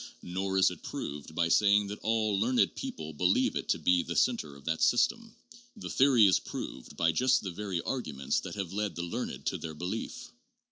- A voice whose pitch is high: No, very low, 95 Hz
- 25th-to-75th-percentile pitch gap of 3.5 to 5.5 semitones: Yes, average, 4.6 semitones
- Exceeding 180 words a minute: Yes, average, 200 wpm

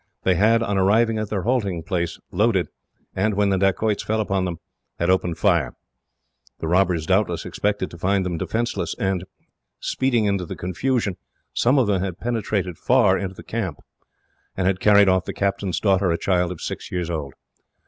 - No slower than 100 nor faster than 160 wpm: No, average, 185 wpm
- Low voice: Yes, very low, 95 Hz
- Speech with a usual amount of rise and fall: Yes, average, 3.0 semitones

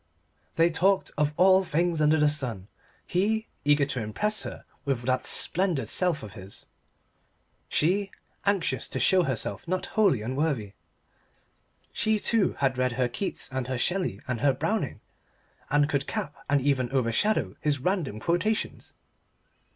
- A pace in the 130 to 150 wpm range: Yes, average, 145 wpm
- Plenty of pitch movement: Yes, wide, 6.3 semitones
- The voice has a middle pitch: Yes, medium, 145 Hz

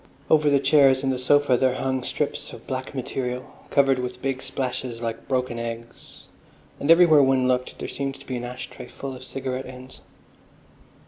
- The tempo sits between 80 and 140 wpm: No, average, 180 wpm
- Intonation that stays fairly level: Yes, narrow, 1.4 semitones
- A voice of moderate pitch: No, low, 130 Hz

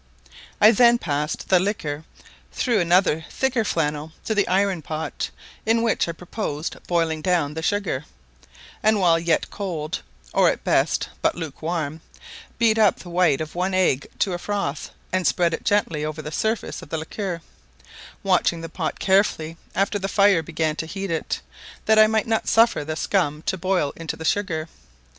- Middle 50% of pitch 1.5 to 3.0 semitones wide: No, average, 4.3 semitones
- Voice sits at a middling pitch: Yes, medium, 175 Hz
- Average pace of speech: Yes, average, 175 wpm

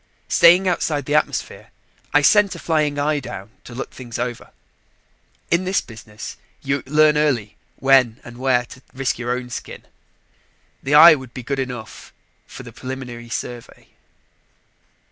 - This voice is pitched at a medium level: No, low, 130 Hz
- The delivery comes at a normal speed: Yes, average, 150 wpm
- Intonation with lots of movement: No, average, 3.7 semitones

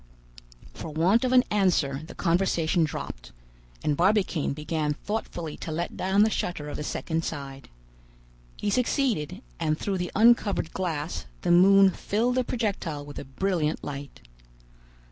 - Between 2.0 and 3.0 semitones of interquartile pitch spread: No, average, 4.9 semitones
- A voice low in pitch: No, medium, 175 Hz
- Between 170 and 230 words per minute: No, average, 145 wpm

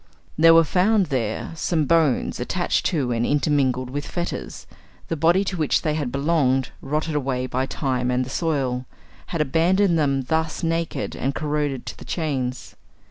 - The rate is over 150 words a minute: Yes, average, 165 wpm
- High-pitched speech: No, medium, 150 Hz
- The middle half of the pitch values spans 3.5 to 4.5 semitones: Yes, average, 4.1 semitones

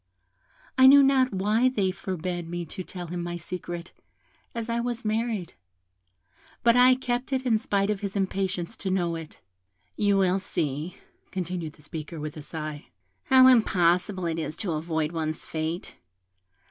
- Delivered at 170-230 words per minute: No, average, 160 wpm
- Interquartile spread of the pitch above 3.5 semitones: Yes, average, 5.1 semitones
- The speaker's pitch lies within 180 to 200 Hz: Yes, medium, 185 Hz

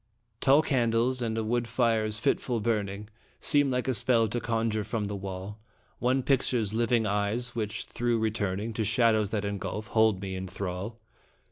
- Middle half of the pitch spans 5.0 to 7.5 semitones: No, narrow, 2.6 semitones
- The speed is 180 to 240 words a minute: No, average, 165 wpm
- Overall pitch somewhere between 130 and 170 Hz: No, low, 110 Hz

